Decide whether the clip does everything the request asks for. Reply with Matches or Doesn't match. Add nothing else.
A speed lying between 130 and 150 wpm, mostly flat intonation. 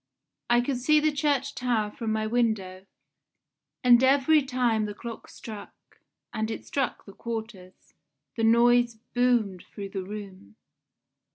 Doesn't match